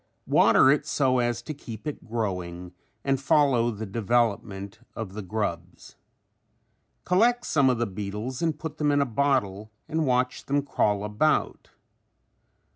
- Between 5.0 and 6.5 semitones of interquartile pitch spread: Yes, average, 5.3 semitones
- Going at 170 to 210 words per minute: No, average, 145 wpm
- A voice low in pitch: Yes, low, 120 Hz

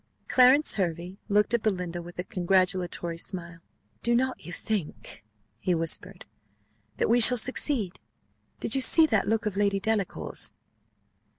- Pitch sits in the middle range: No, high, 195 Hz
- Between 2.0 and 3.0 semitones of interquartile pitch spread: No, average, 4.4 semitones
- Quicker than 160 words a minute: No, average, 140 wpm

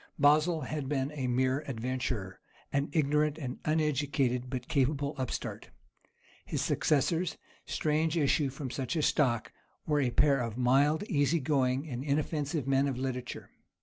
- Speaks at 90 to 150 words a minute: Yes, slow, 135 wpm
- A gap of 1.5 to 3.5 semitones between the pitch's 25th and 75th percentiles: Yes, average, 2.8 semitones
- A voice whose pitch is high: No, medium, 140 Hz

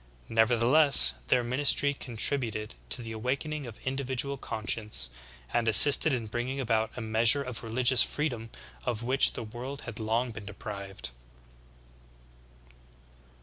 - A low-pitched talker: Yes, low, 120 Hz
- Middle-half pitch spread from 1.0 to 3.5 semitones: Yes, average, 3.1 semitones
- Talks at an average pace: No, slow, 125 wpm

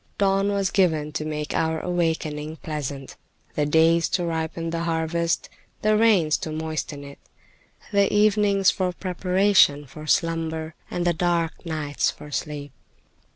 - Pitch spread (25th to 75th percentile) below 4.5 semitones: Yes, average, 2.9 semitones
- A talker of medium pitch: Yes, medium, 165 Hz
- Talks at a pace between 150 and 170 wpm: No, average, 140 wpm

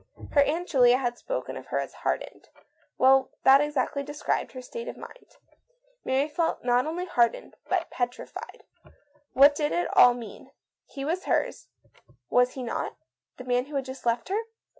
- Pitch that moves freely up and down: No, average, 3.4 semitones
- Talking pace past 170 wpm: No, average, 165 wpm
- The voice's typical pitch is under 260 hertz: No, very high, 270 Hz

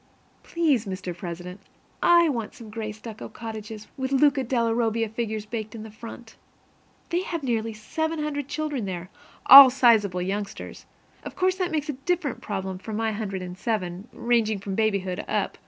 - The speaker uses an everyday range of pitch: Yes, average, 4.7 semitones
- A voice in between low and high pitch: No, high, 225 Hz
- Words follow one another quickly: No, average, 170 wpm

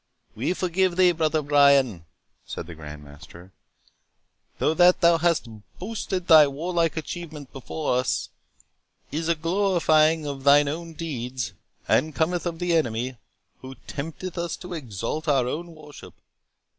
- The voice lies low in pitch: No, medium, 155 Hz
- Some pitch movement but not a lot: Yes, average, 4.4 semitones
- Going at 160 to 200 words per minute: No, average, 140 wpm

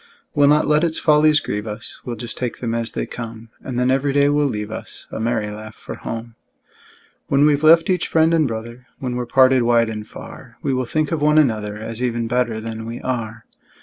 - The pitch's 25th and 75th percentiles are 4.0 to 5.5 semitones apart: Yes, average, 4.3 semitones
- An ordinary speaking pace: No, fast, 220 wpm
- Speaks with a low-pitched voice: Yes, low, 120 Hz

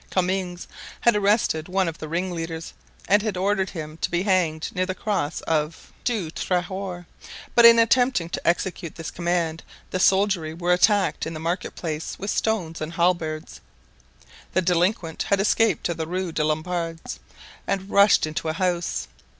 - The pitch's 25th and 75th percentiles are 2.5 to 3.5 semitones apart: Yes, average, 3.0 semitones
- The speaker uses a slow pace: No, average, 165 wpm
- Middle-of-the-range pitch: Yes, medium, 180 Hz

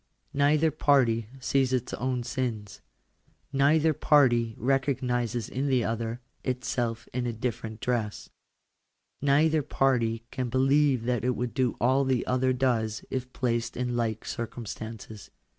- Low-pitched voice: Yes, low, 125 Hz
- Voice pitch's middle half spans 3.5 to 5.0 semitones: No, narrow, 2.5 semitones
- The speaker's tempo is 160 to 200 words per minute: No, average, 140 wpm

